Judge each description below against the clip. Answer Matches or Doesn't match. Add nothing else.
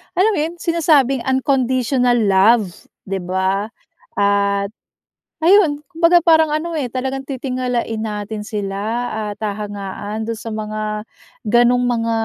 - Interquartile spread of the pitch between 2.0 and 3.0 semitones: Doesn't match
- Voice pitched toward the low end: Doesn't match